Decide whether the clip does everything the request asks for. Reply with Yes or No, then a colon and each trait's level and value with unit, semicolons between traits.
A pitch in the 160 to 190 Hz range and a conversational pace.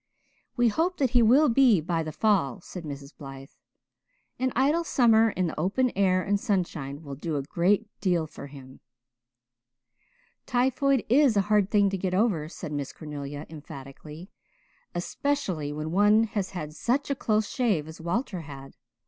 Yes: medium, 185 Hz; average, 165 wpm